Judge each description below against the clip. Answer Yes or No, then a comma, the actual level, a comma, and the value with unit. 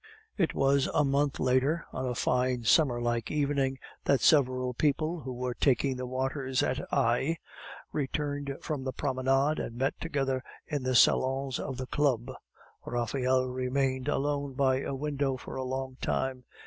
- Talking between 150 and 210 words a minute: Yes, average, 160 wpm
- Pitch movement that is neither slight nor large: No, narrow, 1.7 semitones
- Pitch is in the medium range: No, low, 130 Hz